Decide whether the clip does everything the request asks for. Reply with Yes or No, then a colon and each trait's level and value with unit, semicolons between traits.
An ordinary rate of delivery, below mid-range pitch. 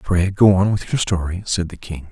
No: fast, 255 wpm; very low, 90 Hz